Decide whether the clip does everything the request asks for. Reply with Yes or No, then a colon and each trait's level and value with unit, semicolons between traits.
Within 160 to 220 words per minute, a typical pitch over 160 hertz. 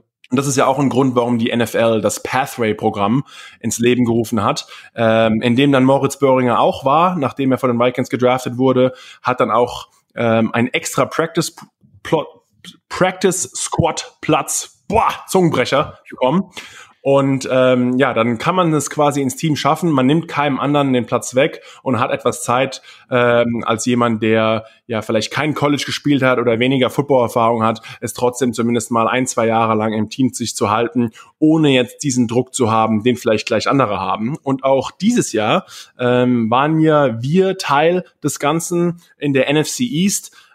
No: average, 175 wpm; low, 125 Hz